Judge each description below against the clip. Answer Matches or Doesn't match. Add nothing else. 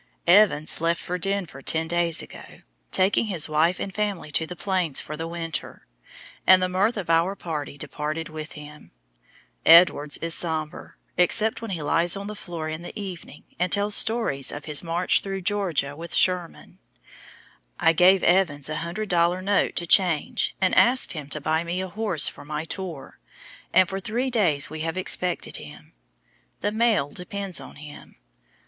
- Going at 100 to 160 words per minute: Doesn't match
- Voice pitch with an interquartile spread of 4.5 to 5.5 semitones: Doesn't match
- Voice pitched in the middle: Matches